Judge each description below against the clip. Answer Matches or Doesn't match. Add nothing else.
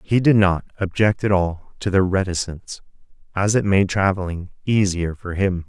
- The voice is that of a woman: Doesn't match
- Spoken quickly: Doesn't match